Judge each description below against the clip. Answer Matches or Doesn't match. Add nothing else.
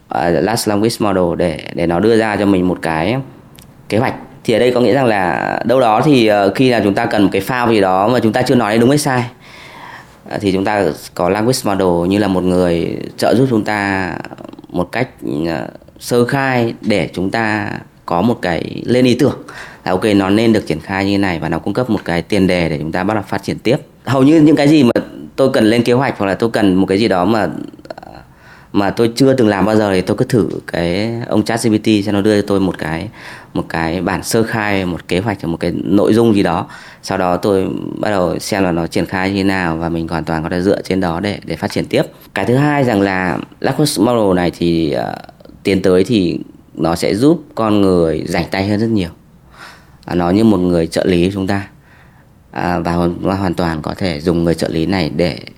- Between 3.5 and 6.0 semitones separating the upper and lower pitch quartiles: Matches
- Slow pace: Doesn't match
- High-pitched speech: Doesn't match